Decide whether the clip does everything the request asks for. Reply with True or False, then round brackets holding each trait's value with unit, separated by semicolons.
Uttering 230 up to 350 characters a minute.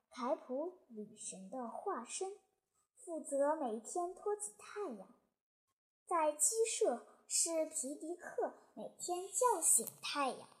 False (160 characters per minute)